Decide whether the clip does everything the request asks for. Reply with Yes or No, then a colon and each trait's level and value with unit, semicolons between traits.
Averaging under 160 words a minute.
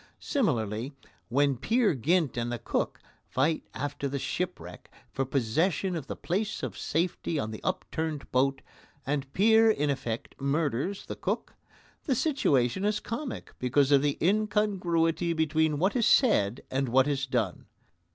Yes: average, 150 wpm